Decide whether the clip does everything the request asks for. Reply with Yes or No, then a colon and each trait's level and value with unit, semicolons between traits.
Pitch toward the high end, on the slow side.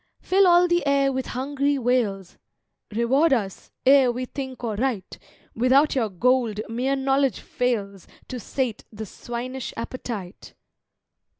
Yes: very high, 255 Hz; slow, 130 wpm